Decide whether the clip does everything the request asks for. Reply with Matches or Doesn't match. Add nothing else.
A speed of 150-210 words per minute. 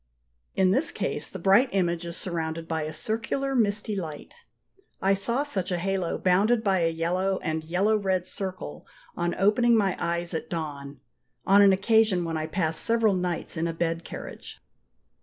Matches